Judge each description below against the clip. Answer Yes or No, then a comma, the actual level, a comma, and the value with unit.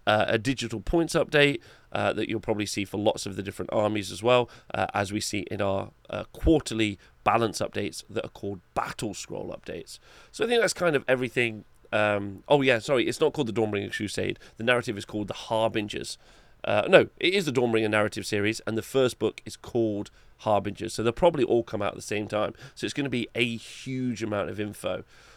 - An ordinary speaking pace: No, fast, 220 wpm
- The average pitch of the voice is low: Yes, low, 110 Hz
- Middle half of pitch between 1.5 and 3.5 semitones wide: Yes, average, 2.8 semitones